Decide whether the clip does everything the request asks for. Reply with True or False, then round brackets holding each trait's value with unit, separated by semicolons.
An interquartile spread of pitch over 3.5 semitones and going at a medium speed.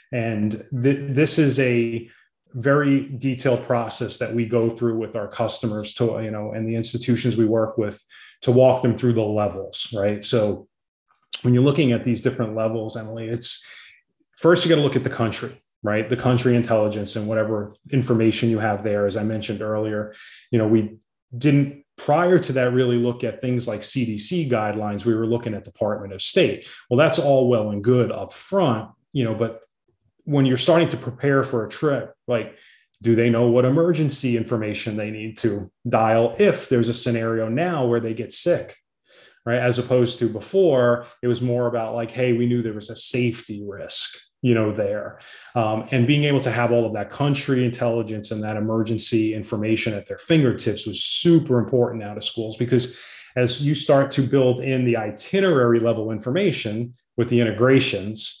False (2.5 semitones; 185 wpm)